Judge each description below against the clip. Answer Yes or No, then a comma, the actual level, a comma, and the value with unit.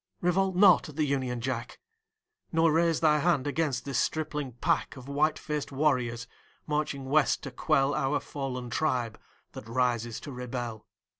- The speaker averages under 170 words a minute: Yes, average, 155 wpm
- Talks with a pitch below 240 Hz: Yes, medium, 140 Hz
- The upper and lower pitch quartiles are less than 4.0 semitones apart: Yes, average, 3.6 semitones